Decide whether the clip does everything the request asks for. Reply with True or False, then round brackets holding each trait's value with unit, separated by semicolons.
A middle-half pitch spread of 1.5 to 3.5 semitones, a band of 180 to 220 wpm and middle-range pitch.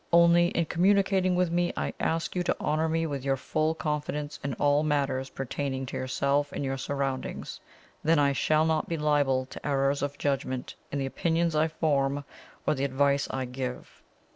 True (3.0 semitones; 185 wpm; 145 Hz)